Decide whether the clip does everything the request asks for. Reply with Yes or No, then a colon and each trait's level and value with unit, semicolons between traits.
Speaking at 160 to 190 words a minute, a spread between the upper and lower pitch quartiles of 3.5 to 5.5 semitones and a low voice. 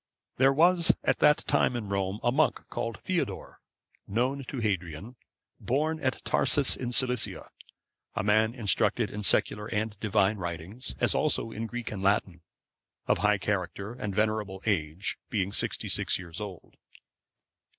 No: average, 150 wpm; average, 4.2 semitones; low, 110 Hz